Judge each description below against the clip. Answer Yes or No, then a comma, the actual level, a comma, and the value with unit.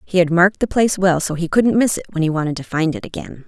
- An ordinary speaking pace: No, fast, 310 wpm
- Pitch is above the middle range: No, medium, 175 Hz